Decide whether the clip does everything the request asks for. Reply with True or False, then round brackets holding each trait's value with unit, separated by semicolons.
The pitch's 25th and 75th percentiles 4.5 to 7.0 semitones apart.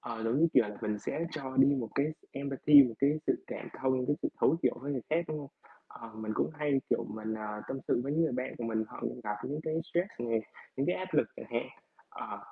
True (4.9 semitones)